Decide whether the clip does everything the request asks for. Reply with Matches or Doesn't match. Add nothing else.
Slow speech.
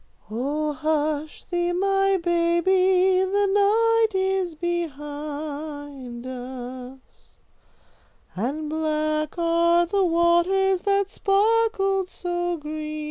Matches